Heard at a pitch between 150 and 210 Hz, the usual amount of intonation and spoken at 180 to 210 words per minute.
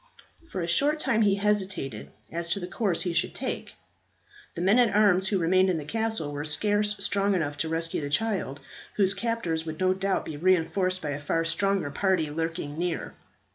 Yes: medium, 185 Hz; average, 3.7 semitones; average, 195 wpm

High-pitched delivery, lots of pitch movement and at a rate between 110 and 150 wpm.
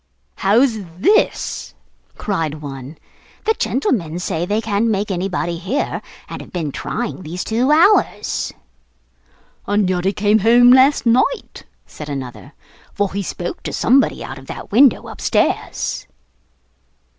Yes: high, 205 Hz; wide, 5.7 semitones; slow, 135 wpm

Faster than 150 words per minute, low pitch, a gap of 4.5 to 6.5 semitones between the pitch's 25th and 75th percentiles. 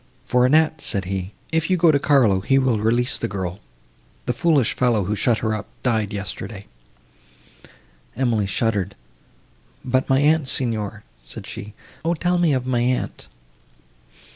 No: average, 140 wpm; low, 120 Hz; average, 4.9 semitones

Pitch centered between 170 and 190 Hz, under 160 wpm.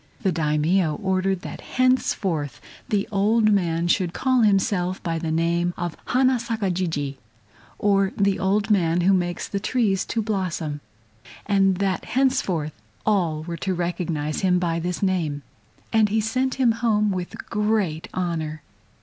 Yes: medium, 185 Hz; average, 150 wpm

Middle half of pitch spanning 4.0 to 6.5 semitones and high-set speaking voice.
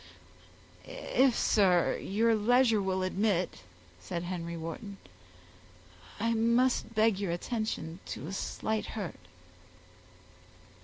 Yes: average, 4.4 semitones; high, 200 Hz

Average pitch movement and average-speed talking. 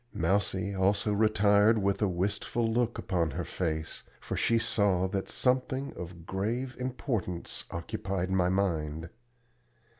No: average, 3.8 semitones; slow, 125 wpm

